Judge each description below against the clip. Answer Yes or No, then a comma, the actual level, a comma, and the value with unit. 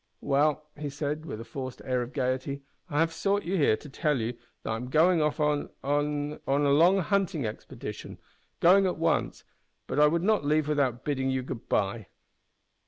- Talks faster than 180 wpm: Yes, average, 190 wpm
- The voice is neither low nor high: Yes, medium, 145 Hz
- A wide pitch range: No, average, 3.5 semitones